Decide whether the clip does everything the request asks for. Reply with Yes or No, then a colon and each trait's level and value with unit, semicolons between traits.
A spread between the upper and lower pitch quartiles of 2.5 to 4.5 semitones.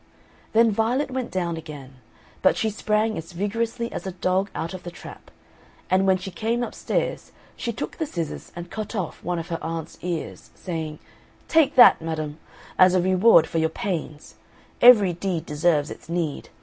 No: average, 4.9 semitones